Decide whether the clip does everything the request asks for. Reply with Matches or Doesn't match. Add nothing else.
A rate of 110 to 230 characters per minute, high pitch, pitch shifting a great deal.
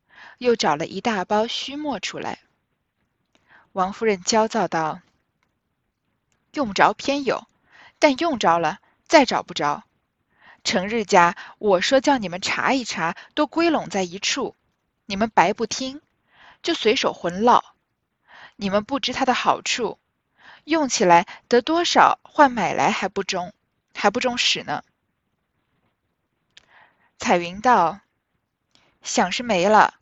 Matches